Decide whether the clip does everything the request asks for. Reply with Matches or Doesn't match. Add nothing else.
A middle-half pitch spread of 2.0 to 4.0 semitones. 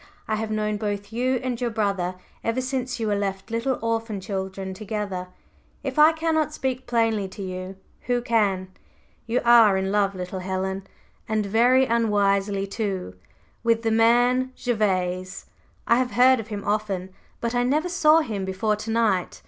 Matches